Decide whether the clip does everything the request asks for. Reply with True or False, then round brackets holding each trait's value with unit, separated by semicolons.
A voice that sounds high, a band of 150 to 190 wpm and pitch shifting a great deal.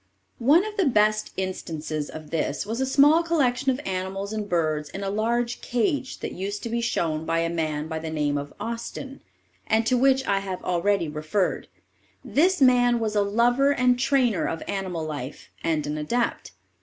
True (205 Hz; 185 wpm; 7.2 semitones)